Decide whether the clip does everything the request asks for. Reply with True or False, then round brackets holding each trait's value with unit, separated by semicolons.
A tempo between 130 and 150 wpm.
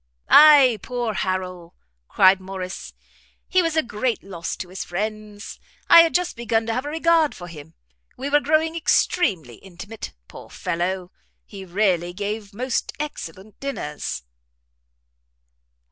True (135 wpm)